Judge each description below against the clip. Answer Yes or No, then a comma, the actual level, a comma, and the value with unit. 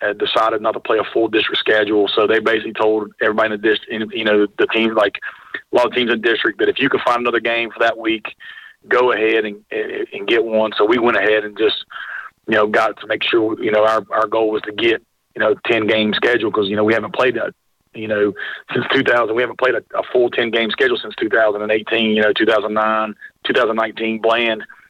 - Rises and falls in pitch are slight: Yes, narrow, 1.2 semitones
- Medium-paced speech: No, fast, 230 wpm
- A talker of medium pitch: No, low, 110 Hz